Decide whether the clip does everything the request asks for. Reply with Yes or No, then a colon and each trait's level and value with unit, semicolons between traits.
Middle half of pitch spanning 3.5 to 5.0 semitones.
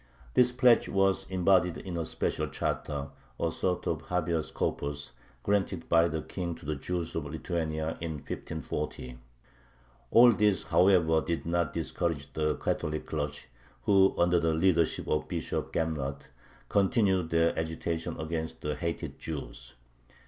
No: average, 2.7 semitones